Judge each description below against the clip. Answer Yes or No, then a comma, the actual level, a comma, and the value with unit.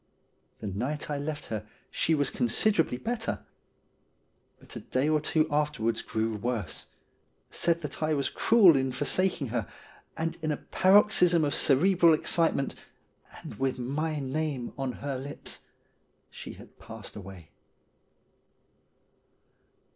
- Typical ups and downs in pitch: Yes, average, 4.3 semitones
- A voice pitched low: No, medium, 145 Hz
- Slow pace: Yes, slow, 130 wpm